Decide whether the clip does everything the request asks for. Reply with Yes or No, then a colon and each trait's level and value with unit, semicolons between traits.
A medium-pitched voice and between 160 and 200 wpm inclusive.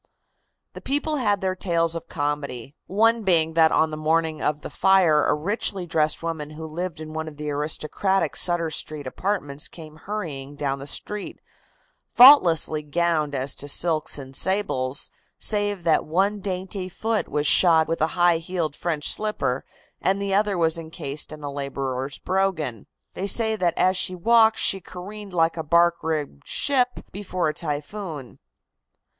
Yes: medium, 165 Hz; average, 165 wpm